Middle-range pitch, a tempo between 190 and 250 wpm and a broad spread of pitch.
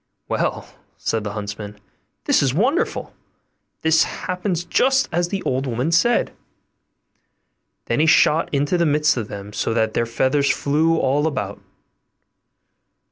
No: medium, 145 Hz; slow, 135 wpm; wide, 6.4 semitones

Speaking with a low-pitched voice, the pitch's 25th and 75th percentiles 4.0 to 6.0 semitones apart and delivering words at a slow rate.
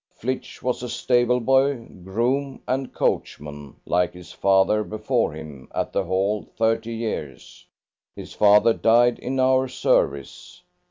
Yes: low, 115 Hz; average, 5.0 semitones; slow, 130 wpm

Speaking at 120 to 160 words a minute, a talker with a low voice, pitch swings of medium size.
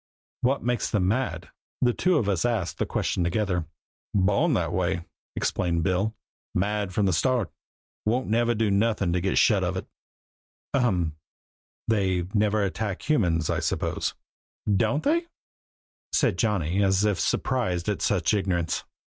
Yes: average, 150 wpm; low, 100 Hz; average, 4.1 semitones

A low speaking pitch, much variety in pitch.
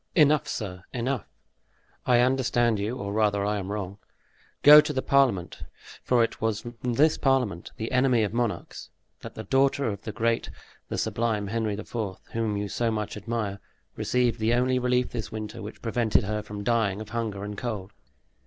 No: low, 115 Hz; average, 3.1 semitones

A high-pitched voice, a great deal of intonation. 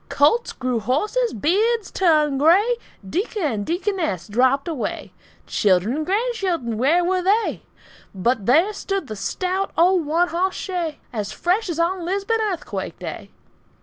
Yes: very high, 345 Hz; wide, 6.8 semitones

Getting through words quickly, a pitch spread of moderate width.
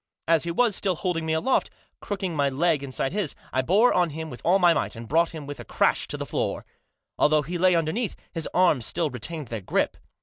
Yes: fast, 230 wpm; average, 3.8 semitones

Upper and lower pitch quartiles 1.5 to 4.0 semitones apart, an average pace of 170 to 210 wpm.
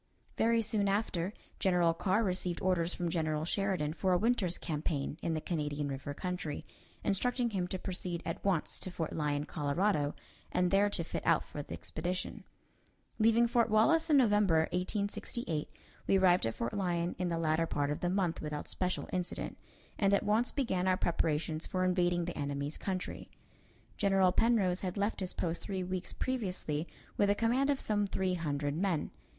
Yes: average, 3.7 semitones; average, 175 wpm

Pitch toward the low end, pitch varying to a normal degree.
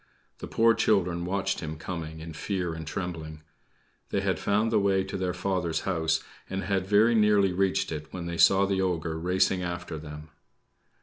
Yes: very low, 90 Hz; average, 3.1 semitones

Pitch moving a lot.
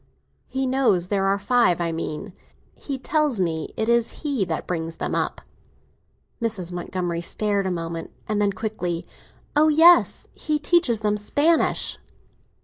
Yes: wide, 7.0 semitones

